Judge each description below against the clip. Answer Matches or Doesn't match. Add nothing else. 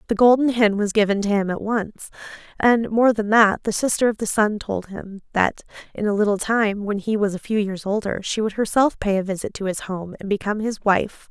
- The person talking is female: Matches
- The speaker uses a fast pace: Matches